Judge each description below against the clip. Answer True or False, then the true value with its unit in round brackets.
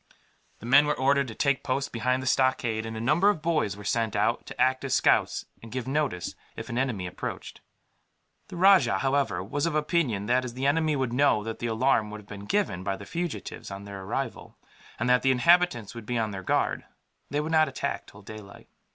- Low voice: True (125 Hz)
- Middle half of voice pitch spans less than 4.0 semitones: False (4.8 semitones)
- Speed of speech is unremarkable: False (220 wpm)